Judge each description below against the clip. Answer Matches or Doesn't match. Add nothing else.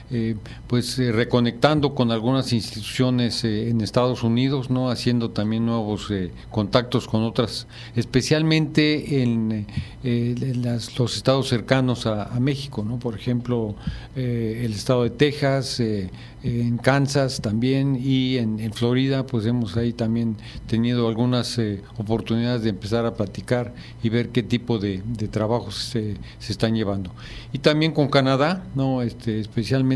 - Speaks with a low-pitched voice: Matches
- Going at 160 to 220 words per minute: Doesn't match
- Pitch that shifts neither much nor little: Doesn't match